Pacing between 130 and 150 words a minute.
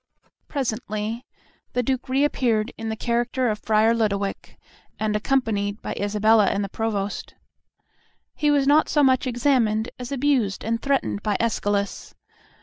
Yes: average, 145 wpm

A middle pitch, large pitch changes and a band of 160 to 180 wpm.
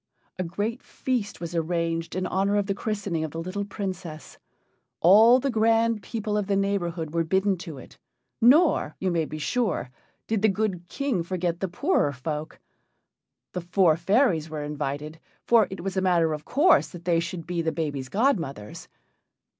No: medium, 180 Hz; average, 4.2 semitones; average, 175 wpm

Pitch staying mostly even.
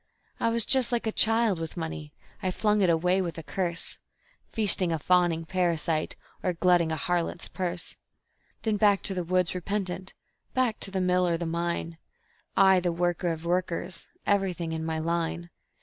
Yes: narrow, 2.3 semitones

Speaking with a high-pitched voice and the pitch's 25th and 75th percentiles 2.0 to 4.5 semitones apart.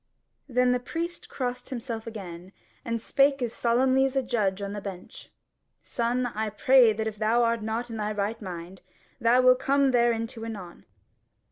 Yes: high, 230 Hz; average, 3.0 semitones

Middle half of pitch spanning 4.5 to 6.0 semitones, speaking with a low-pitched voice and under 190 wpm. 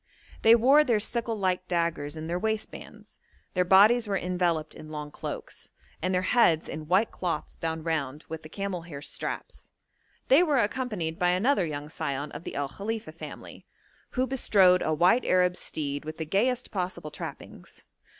No: wide, 5.6 semitones; medium, 180 Hz; average, 170 wpm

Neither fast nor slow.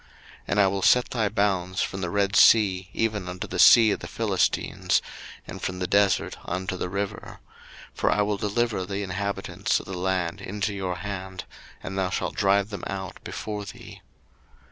Yes: average, 185 wpm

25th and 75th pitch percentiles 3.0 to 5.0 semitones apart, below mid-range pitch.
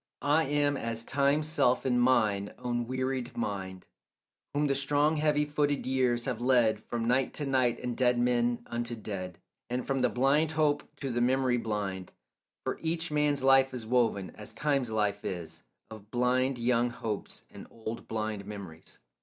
Yes: average, 3.5 semitones; low, 125 Hz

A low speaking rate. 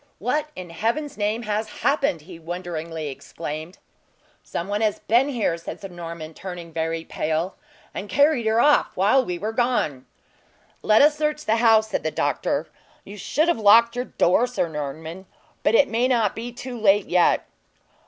No: average, 175 wpm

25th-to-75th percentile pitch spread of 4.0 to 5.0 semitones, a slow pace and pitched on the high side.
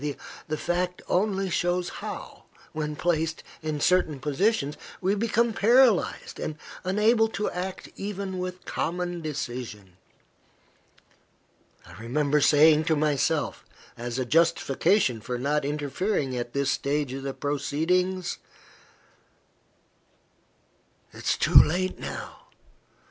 No: average, 4.5 semitones; slow, 110 wpm; medium, 160 Hz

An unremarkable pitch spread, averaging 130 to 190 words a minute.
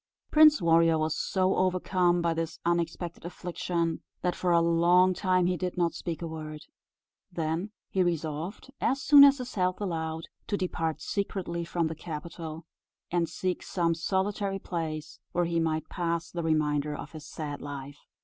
No: narrow, 2.2 semitones; average, 165 wpm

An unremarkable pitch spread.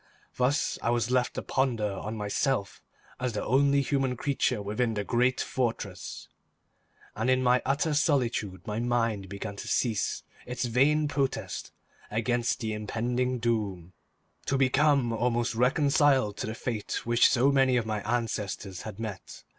Yes: average, 3.3 semitones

